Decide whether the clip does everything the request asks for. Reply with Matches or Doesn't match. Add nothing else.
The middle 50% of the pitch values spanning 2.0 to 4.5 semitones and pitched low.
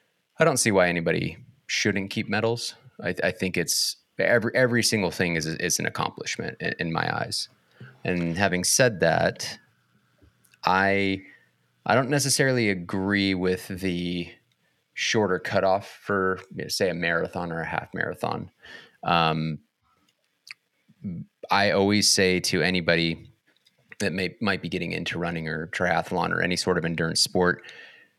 Matches